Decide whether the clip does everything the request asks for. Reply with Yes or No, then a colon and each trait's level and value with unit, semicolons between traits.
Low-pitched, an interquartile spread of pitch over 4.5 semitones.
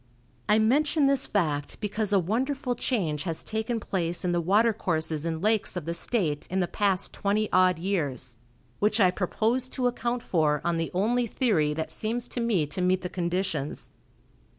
No: high, 190 Hz; average, 5.2 semitones